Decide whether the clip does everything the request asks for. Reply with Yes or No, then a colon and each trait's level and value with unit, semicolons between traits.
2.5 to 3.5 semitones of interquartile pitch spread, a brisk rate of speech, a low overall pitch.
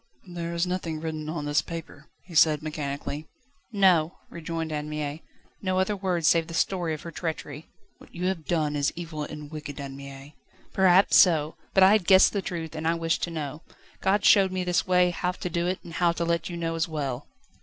No: average, 2.8 semitones; fast, 215 wpm; medium, 165 Hz